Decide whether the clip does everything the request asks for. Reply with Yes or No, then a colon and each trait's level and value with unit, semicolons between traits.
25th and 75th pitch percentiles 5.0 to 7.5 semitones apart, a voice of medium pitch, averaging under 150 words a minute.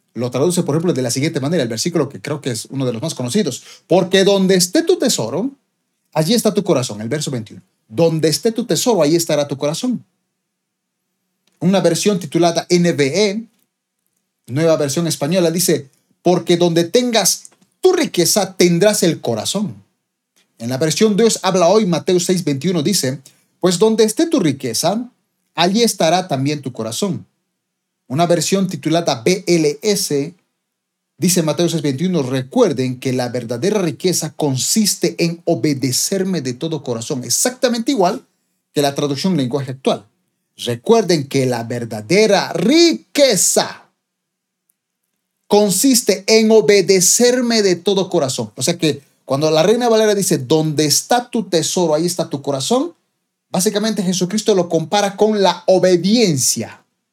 Yes: wide, 5.5 semitones; medium, 175 Hz; average, 140 wpm